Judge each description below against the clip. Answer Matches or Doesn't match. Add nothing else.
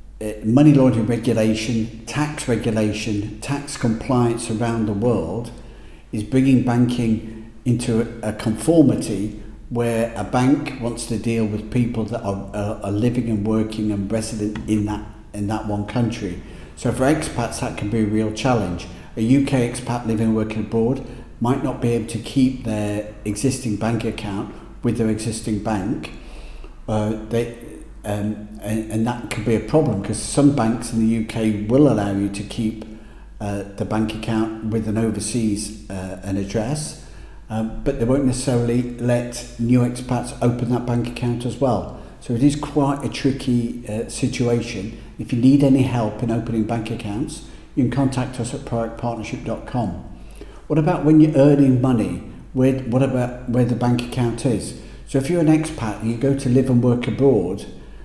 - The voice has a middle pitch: Doesn't match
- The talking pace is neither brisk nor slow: Matches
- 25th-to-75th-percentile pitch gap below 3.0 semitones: Matches